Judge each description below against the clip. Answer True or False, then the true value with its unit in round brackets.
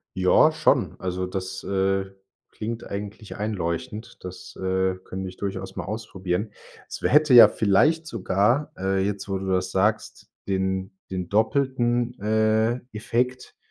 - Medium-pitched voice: False (100 Hz)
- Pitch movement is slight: False (3.2 semitones)